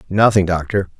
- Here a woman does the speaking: No, male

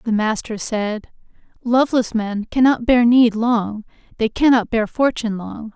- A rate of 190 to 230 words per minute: No, average, 145 wpm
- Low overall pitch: No, high, 230 Hz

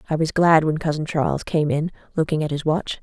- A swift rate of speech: Yes, fast, 240 wpm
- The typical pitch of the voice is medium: Yes, medium, 155 Hz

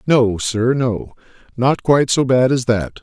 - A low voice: Yes, low, 125 Hz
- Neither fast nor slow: Yes, average, 180 wpm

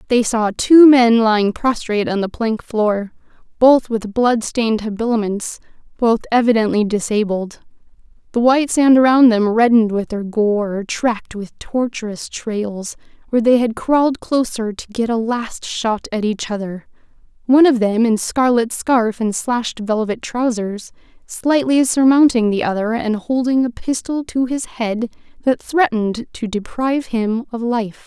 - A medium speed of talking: Yes, average, 150 wpm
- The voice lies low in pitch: No, high, 230 Hz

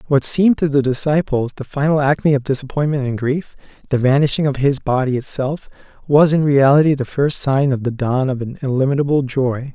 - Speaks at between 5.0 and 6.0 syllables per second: Yes, 5.6 syllables/s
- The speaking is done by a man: Yes, male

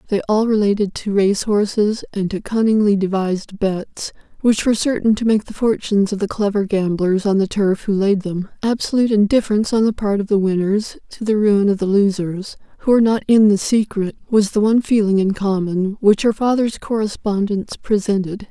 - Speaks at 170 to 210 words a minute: Yes, average, 190 wpm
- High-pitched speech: Yes, high, 205 Hz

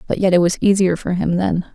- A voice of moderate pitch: Yes, medium, 180 Hz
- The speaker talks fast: Yes, fast, 275 wpm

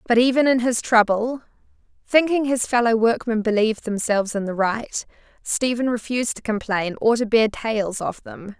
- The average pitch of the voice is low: No, high, 230 Hz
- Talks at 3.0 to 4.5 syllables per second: No, 5.0 syllables/s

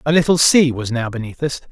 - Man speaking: Yes, male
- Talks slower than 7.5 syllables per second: Yes, 5.9 syllables/s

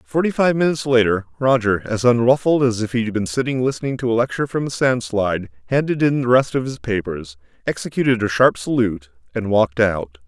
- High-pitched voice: No, low, 115 Hz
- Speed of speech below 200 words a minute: No, fast, 205 wpm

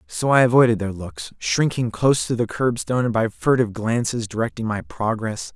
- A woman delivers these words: No, male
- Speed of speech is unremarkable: Yes, average, 185 wpm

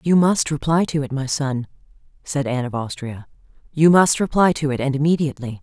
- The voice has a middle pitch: Yes, medium, 145 Hz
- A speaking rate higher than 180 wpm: Yes, average, 190 wpm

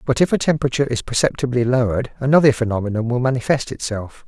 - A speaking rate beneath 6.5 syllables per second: No, 7.0 syllables/s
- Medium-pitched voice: No, low, 125 Hz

